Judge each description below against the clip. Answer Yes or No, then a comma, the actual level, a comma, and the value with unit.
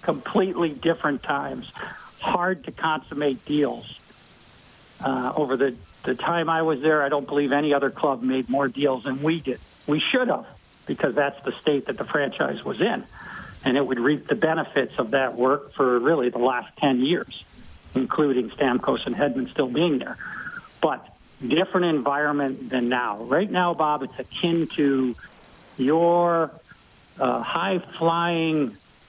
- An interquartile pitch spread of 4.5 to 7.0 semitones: No, average, 3.6 semitones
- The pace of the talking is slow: No, average, 155 wpm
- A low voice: No, medium, 145 Hz